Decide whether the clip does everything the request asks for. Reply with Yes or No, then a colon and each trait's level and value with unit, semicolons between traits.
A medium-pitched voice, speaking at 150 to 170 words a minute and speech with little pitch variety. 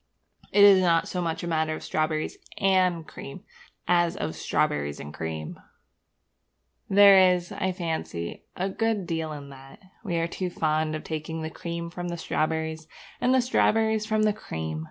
No: medium, 170 Hz; average, 160 wpm; average, 3.3 semitones